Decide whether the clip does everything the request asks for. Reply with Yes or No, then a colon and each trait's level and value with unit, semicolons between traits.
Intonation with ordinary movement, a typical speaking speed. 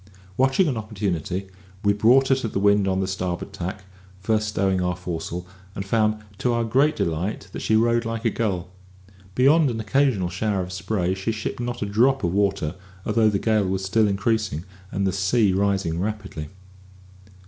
Yes: average, 3.2 semitones; average, 180 wpm